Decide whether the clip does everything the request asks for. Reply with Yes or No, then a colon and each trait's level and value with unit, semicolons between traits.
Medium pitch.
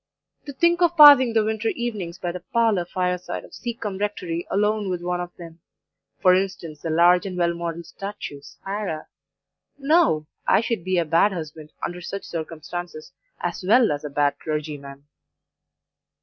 Yes: medium, 180 Hz